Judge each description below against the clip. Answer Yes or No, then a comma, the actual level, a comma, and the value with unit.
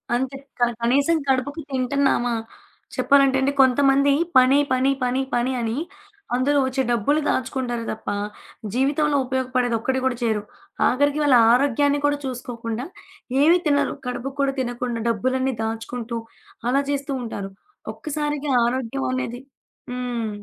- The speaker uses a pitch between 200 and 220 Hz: No, very high, 260 Hz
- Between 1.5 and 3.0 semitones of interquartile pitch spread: Yes, narrow, 2.5 semitones